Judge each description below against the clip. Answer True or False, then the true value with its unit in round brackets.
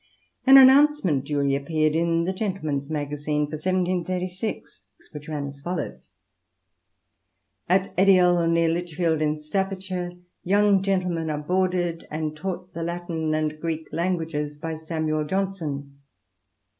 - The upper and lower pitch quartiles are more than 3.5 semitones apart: False (3.2 semitones)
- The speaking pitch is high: False (165 Hz)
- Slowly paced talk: True (125 wpm)